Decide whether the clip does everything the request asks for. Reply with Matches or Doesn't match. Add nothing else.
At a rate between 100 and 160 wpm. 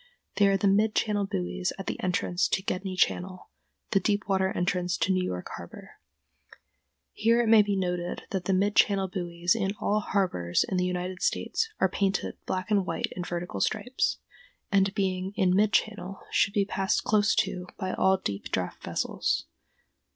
Doesn't match